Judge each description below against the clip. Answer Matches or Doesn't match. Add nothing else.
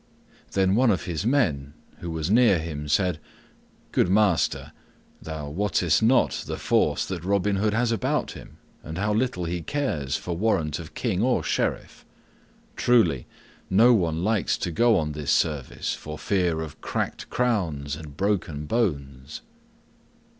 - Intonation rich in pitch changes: Matches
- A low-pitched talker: Matches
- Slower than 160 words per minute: Matches